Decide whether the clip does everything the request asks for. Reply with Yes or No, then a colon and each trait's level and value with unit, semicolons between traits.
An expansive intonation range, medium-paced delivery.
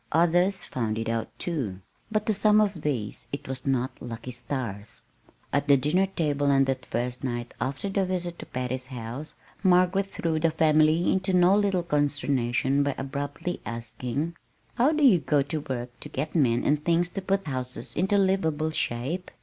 Yes: wide, 5.8 semitones; average, 175 wpm